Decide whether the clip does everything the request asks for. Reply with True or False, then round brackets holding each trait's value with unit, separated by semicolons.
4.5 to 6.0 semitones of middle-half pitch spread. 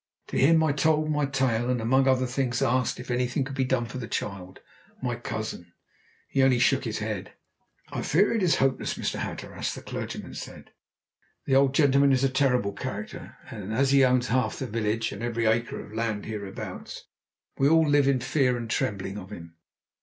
False (3.5 semitones)